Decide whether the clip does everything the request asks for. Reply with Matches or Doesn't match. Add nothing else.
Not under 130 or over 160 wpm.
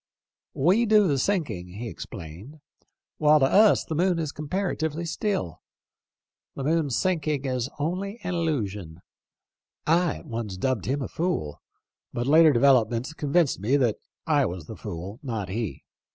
Matches